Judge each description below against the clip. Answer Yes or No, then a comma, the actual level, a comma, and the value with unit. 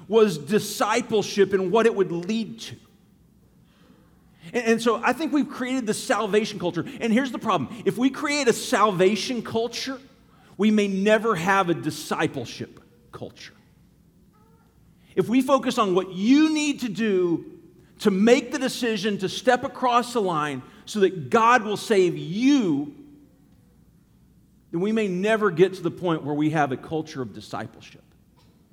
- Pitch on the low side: No, high, 210 Hz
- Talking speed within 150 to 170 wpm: Yes, average, 155 wpm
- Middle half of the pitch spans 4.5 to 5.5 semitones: Yes, average, 5.2 semitones